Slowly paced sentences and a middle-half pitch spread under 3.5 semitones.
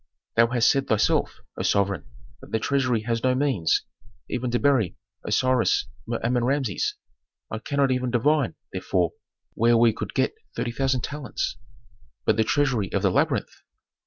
No: average, 160 wpm; average, 3.1 semitones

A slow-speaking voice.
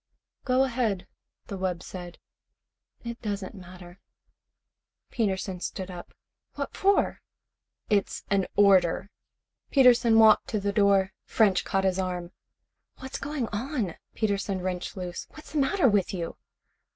Yes: slow, 125 wpm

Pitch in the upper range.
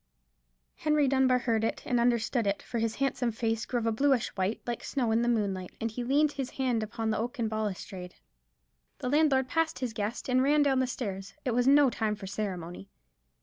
Yes: high, 235 Hz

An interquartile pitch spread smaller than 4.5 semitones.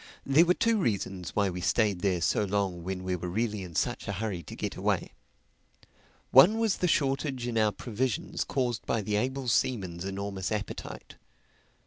No: wide, 5.5 semitones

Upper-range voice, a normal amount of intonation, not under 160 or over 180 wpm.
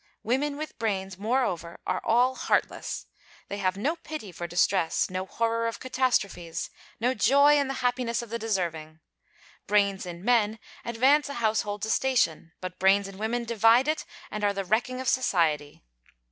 Yes: high, 220 Hz; average, 5.0 semitones; average, 165 wpm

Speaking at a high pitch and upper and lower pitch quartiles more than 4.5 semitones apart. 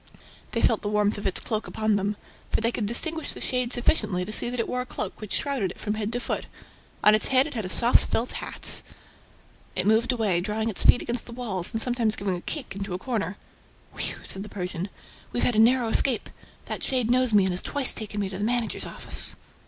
No: high, 220 Hz; average, 3.3 semitones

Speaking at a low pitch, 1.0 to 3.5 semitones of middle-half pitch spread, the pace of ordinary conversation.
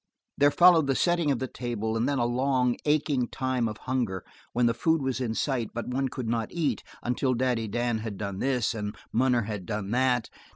No: low, 125 Hz; average, 2.9 semitones; fast, 210 wpm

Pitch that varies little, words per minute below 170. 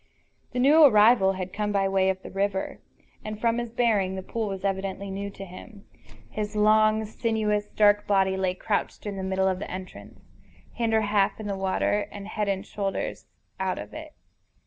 No: narrow, 2.1 semitones; average, 190 wpm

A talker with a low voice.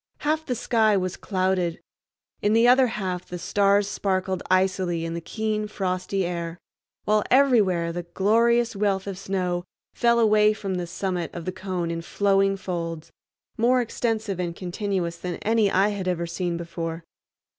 No: high, 190 Hz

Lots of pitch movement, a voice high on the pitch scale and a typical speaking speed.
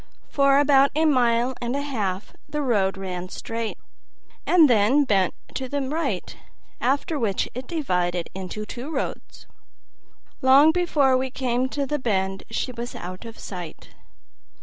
Yes: wide, 5.8 semitones; very high, 250 Hz; average, 150 wpm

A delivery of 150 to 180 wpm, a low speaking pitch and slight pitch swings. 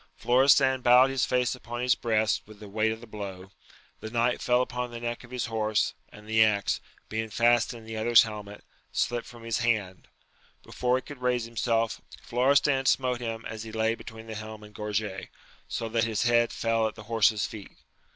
No: average, 200 wpm; low, 115 Hz; narrow, 2.0 semitones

